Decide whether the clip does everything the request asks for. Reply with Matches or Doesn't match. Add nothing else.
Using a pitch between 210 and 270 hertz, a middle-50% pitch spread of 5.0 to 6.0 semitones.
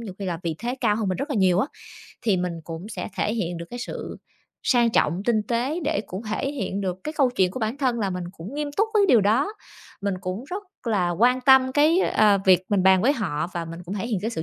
Matches